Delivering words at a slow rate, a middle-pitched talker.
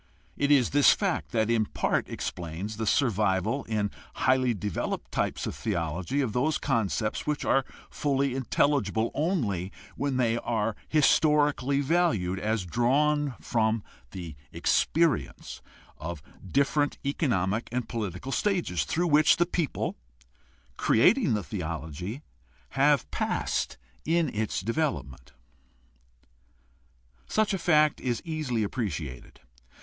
No: slow, 115 wpm; low, 120 Hz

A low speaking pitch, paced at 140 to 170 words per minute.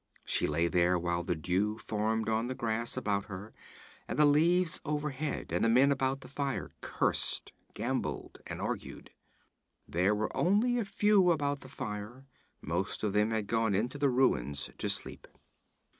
Yes: low, 115 Hz; average, 165 wpm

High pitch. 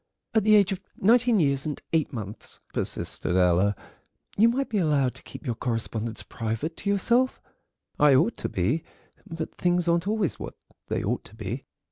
No: medium, 155 Hz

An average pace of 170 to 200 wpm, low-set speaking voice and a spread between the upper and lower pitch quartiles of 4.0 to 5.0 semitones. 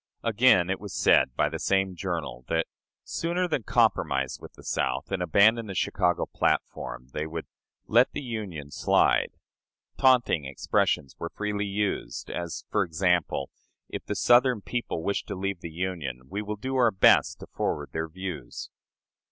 No: average, 160 wpm; very low, 95 Hz; average, 4.6 semitones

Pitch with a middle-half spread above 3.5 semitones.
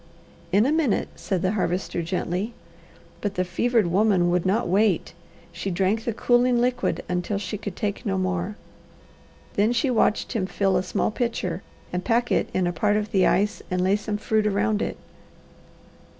No: average, 3.2 semitones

